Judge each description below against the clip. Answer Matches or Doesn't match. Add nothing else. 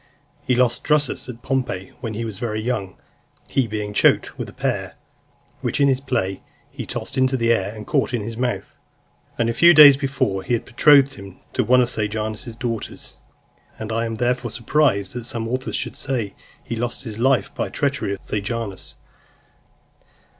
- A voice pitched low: Matches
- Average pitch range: Matches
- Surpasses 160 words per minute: Matches